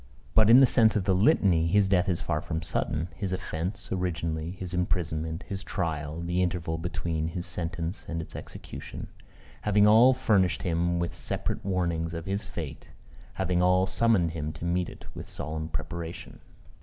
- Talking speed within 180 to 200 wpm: No, average, 170 wpm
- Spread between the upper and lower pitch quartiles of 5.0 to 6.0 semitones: No, average, 2.7 semitones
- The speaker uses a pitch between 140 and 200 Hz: No, very low, 85 Hz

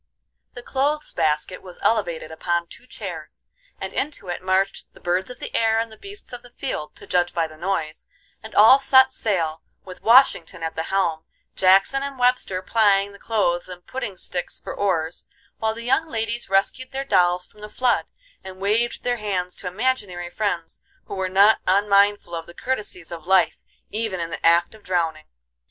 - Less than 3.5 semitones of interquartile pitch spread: No, average, 4.6 semitones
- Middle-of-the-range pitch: No, high, 195 Hz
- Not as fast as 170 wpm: No, average, 185 wpm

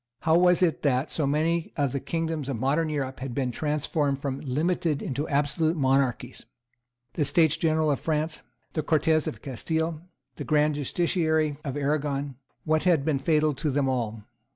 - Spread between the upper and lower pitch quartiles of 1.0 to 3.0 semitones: Yes, narrow, 2.6 semitones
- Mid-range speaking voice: Yes, medium, 150 Hz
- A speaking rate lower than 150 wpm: No, average, 170 wpm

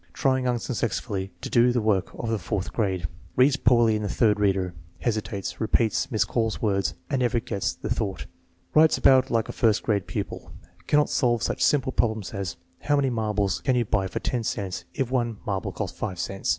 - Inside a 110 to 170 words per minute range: No, average, 190 wpm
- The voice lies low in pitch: Yes, low, 110 Hz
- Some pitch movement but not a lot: Yes, average, 3.7 semitones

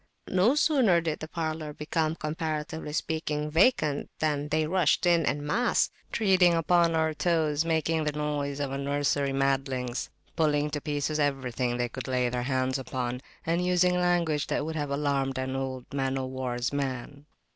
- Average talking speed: Yes, average, 165 wpm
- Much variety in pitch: No, average, 3.1 semitones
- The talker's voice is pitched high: No, medium, 150 Hz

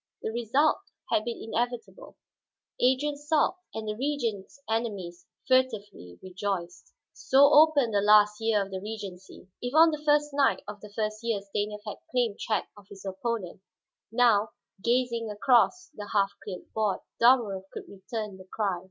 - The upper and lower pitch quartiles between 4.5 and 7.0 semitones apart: No, average, 3.9 semitones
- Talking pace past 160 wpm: No, average, 155 wpm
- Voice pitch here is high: Yes, high, 220 Hz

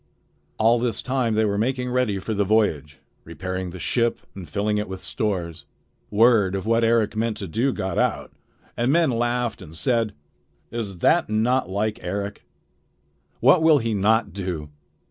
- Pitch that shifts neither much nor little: Yes, average, 3.6 semitones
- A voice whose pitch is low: Yes, low, 110 Hz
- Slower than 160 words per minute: No, average, 165 wpm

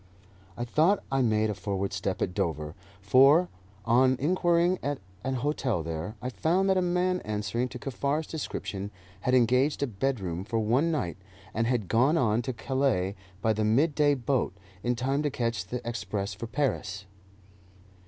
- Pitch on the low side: Yes, low, 125 Hz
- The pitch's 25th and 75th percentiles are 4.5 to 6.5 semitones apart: Yes, wide, 5.4 semitones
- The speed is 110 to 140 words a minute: No, average, 165 wpm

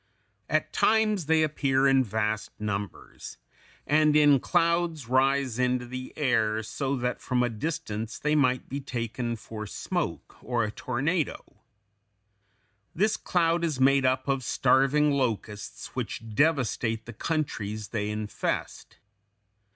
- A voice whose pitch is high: No, low, 130 Hz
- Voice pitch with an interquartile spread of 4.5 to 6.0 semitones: Yes, average, 5.0 semitones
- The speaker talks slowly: Yes, slow, 130 wpm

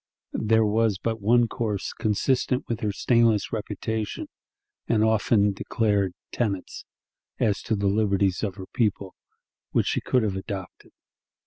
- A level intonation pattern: Yes, narrow, 2.2 semitones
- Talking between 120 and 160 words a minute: Yes, slow, 135 wpm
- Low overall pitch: Yes, low, 105 Hz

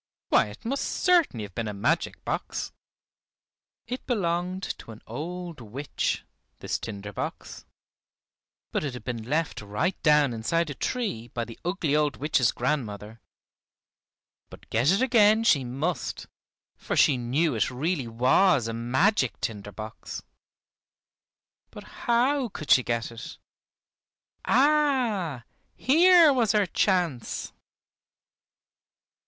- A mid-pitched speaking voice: Yes, medium, 150 Hz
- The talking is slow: Yes, slow, 125 wpm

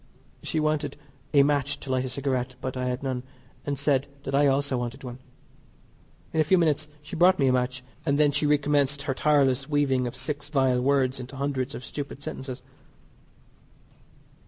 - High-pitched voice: No, medium, 140 Hz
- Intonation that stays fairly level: Yes, narrow, 2.1 semitones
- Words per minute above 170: Yes, average, 180 wpm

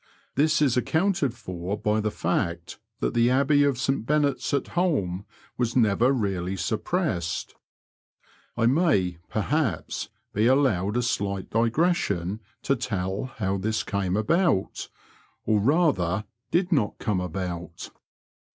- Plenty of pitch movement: Yes, wide, 6.7 semitones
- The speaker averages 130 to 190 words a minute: Yes, slow, 135 wpm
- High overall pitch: No, low, 110 Hz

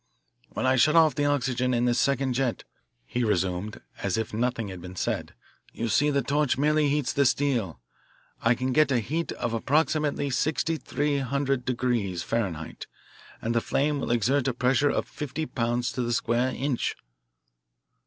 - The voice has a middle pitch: No, low, 125 Hz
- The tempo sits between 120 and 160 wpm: No, average, 175 wpm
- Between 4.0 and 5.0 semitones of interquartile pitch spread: No, average, 3.5 semitones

